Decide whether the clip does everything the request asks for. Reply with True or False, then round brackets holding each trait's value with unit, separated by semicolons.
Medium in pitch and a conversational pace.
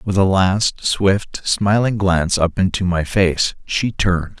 False (95 Hz; 165 wpm)